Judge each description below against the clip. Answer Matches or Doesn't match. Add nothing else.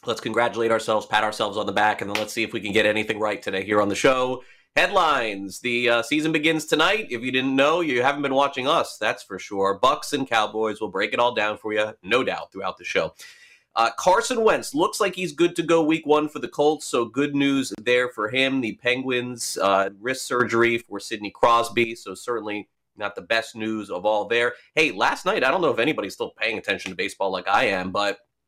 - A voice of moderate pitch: Doesn't match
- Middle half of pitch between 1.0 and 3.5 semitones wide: Doesn't match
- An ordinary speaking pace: Doesn't match